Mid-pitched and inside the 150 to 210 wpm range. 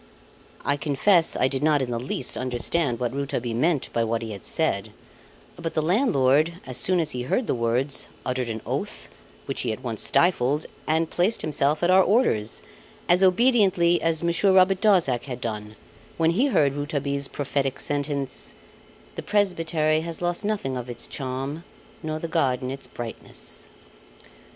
Yes: medium, 145 Hz; average, 165 wpm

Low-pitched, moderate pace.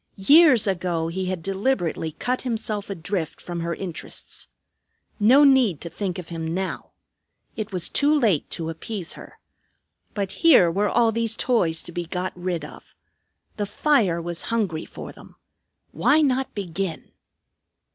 No: high, 190 Hz; average, 150 wpm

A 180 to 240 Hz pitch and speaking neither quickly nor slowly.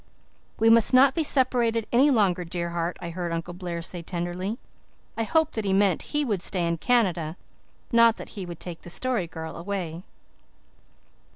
Yes: high, 190 Hz; average, 180 wpm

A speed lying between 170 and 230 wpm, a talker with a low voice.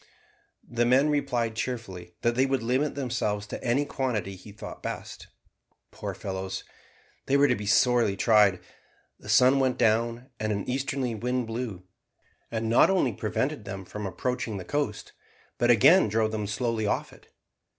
No: average, 160 wpm; low, 115 Hz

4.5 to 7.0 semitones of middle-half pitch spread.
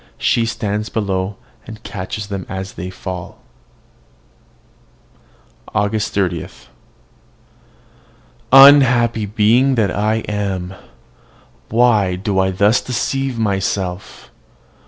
No: average, 3.2 semitones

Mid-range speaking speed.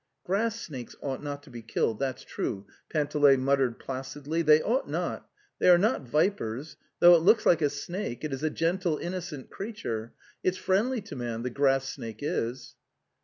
Yes: average, 180 wpm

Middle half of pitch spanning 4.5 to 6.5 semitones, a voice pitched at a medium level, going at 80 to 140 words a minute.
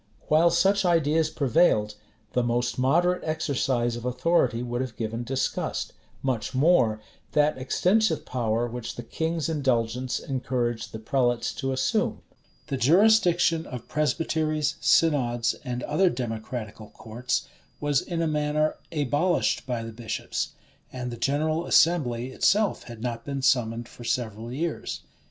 No: average, 4.8 semitones; low, 130 Hz; slow, 135 wpm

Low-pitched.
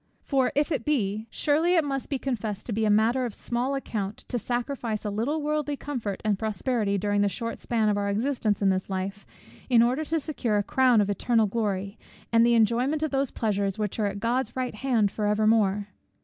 No: high, 225 Hz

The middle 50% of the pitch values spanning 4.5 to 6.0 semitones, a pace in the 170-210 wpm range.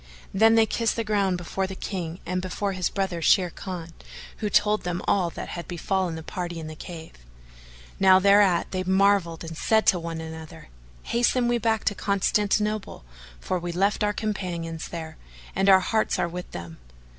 No: average, 3.2 semitones; average, 180 wpm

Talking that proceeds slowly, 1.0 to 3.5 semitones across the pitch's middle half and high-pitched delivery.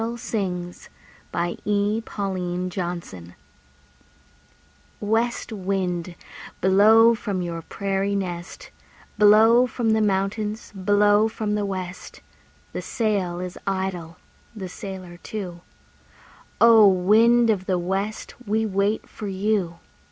Yes: slow, 105 wpm; average, 3.1 semitones; high, 195 Hz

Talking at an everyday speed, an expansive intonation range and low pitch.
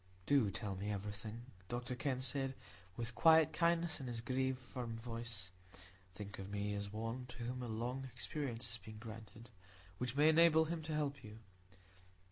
No: average, 170 wpm; average, 3.7 semitones; low, 120 Hz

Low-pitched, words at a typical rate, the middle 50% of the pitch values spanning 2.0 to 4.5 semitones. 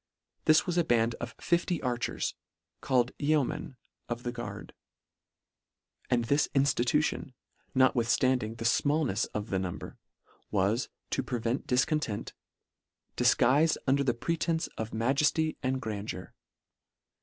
No: low, 125 Hz; slow, 120 wpm; average, 3.9 semitones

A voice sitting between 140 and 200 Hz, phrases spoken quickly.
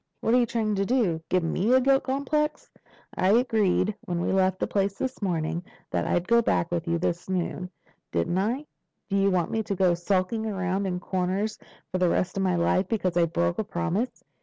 Yes: high, 190 Hz; fast, 210 wpm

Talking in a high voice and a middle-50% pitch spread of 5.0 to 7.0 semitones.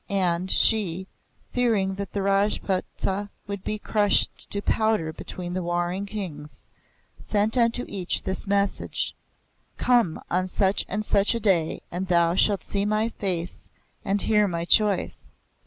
No: high, 195 Hz; average, 2.7 semitones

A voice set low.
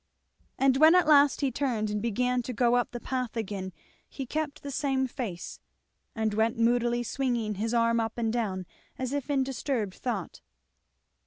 No: high, 240 Hz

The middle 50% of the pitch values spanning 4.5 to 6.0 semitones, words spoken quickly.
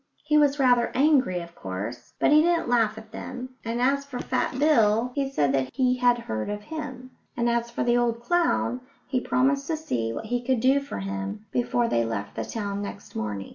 Yes: average, 5.1 semitones; fast, 215 wpm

